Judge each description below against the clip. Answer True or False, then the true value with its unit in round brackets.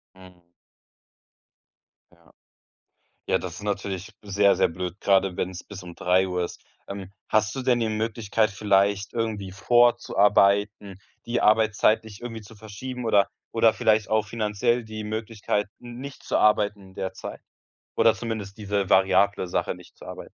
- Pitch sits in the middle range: False (105 Hz)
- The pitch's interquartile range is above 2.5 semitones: False (2.2 semitones)